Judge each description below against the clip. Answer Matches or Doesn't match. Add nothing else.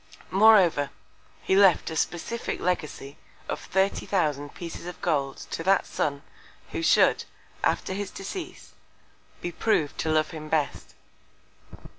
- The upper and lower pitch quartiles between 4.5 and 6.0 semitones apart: Doesn't match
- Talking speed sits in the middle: Doesn't match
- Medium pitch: Matches